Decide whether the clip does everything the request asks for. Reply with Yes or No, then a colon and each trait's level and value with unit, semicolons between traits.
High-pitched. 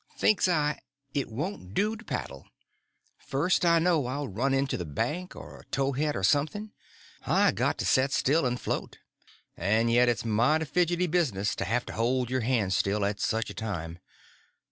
No: low, 130 Hz